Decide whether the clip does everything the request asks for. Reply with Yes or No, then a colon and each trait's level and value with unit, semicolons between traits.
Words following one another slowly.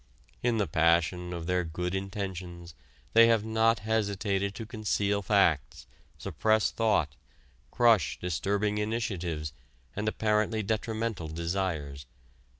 Yes: slow, 110 wpm